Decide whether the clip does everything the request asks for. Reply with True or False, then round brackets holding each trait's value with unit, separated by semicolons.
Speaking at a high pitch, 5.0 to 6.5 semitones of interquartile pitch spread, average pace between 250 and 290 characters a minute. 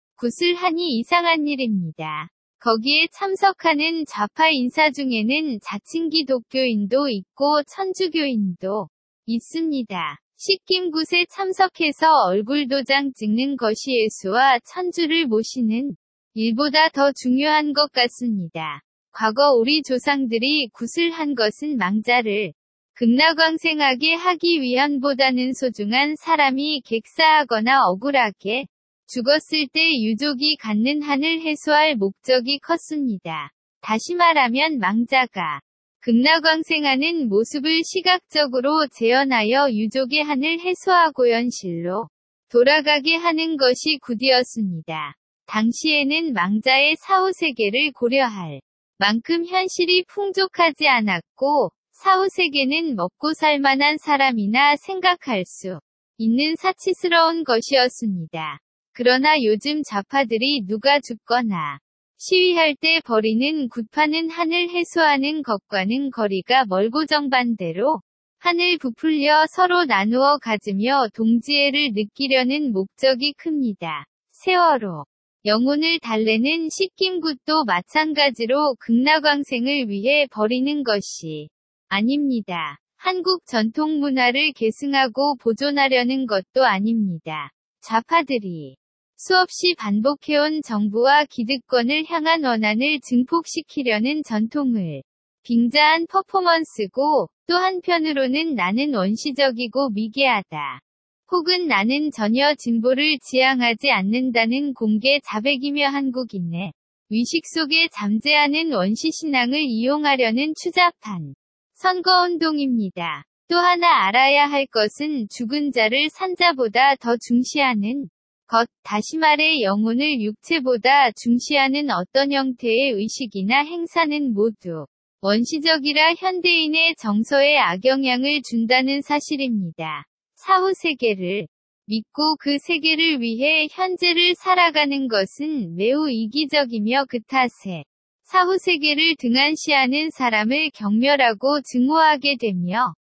True (275 Hz; 5.4 semitones; 260 characters per minute)